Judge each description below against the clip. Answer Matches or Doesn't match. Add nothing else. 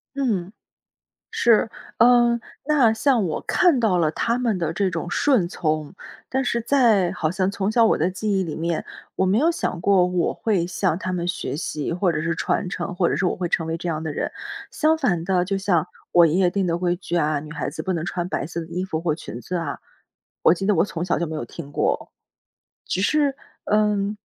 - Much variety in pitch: Doesn't match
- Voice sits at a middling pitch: Matches